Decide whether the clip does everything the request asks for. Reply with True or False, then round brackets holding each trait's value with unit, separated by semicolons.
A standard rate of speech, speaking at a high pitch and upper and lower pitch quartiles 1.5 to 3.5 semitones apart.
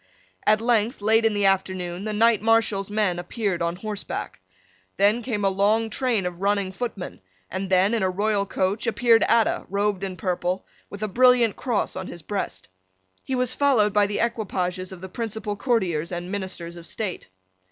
True (180 wpm; 205 Hz; 3.1 semitones)